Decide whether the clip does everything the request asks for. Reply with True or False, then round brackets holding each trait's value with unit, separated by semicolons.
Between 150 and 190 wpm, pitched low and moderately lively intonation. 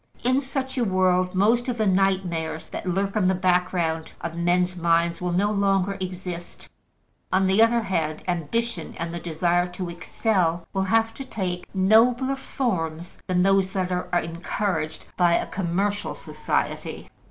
False (155 wpm; 185 Hz; 3.0 semitones)